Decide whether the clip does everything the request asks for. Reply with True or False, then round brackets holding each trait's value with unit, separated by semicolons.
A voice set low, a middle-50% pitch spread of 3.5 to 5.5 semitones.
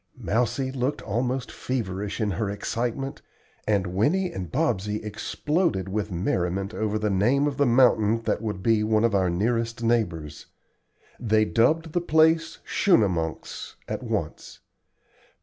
True (110 Hz; 4.7 semitones)